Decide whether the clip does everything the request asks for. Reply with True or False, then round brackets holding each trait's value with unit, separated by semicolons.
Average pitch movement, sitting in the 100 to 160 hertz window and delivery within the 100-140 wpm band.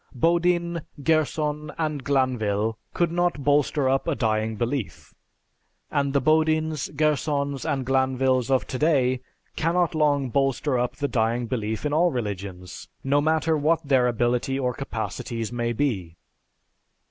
True (4.0 semitones; 135 Hz; 135 wpm)